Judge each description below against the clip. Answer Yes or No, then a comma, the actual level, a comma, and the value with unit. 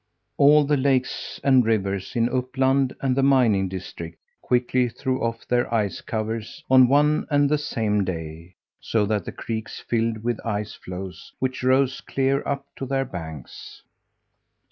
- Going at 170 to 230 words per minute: No, average, 155 wpm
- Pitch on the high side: No, low, 120 Hz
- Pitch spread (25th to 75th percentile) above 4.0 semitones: Yes, average, 4.4 semitones